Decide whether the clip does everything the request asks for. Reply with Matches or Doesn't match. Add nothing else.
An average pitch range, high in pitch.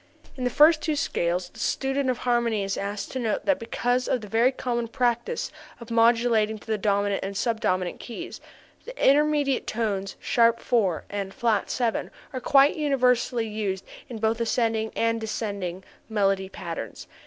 Matches